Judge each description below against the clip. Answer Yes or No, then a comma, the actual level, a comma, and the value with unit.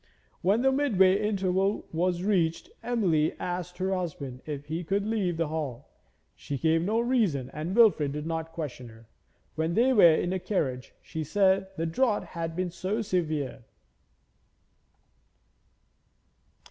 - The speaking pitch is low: No, medium, 175 Hz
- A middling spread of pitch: Yes, average, 4.1 semitones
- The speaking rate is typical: Yes, average, 145 wpm